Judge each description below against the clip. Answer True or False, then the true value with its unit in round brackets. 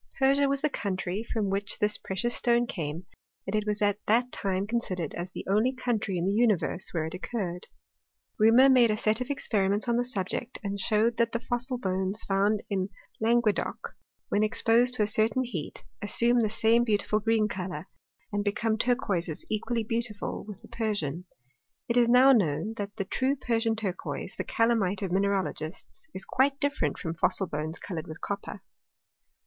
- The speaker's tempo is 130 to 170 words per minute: False (180 wpm)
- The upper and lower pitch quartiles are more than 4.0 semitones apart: False (3.7 semitones)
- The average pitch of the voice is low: False (215 Hz)